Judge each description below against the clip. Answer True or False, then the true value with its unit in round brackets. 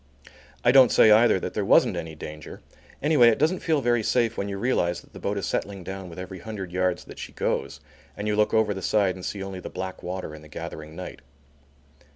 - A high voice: False (95 Hz)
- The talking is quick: True (230 wpm)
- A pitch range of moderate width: True (3.6 semitones)